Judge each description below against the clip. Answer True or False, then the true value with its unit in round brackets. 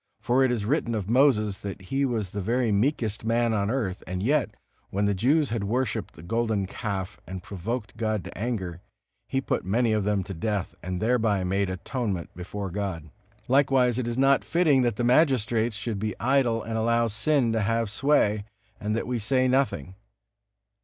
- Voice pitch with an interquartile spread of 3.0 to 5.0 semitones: True (3.8 semitones)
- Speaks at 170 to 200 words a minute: True (185 wpm)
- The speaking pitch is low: True (110 Hz)